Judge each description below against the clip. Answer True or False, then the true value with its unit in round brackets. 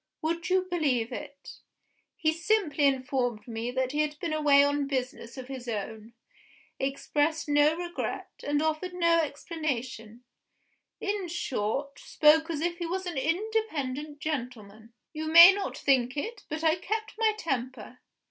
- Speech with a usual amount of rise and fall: True (4.6 semitones)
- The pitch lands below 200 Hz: False (295 Hz)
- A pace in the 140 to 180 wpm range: True (150 wpm)